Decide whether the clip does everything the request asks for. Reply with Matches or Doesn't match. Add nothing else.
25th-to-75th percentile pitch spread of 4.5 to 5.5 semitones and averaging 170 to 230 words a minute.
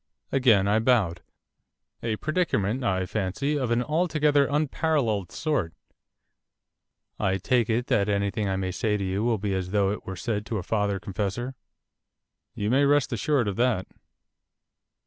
Doesn't match